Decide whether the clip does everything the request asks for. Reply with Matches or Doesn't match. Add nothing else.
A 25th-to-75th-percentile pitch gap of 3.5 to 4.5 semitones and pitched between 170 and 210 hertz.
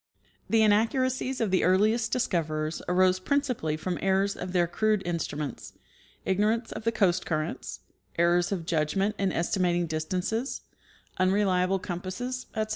Matches